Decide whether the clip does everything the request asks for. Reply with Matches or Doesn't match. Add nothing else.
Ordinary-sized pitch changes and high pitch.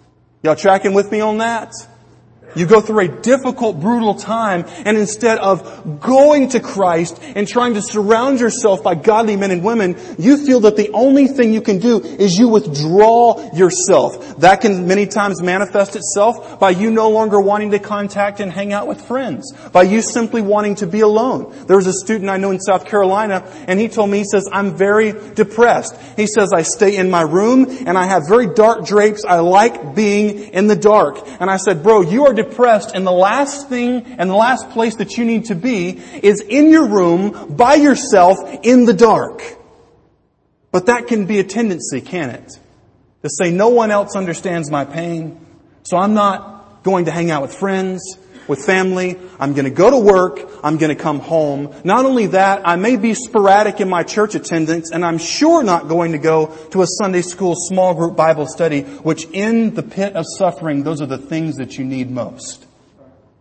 Matches